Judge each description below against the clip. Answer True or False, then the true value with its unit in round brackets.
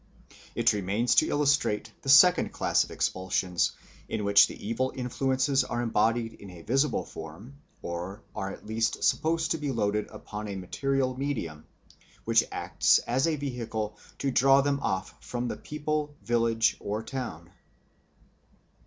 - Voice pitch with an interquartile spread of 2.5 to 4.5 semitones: False (5.0 semitones)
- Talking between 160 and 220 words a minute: False (150 wpm)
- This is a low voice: True (120 Hz)